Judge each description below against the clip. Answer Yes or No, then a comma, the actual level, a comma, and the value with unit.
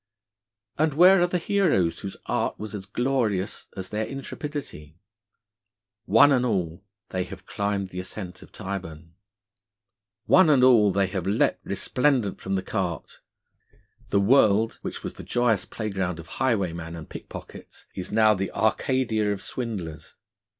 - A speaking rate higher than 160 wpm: No, average, 145 wpm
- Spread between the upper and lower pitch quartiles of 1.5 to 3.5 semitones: No, average, 5.2 semitones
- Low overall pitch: Yes, low, 105 Hz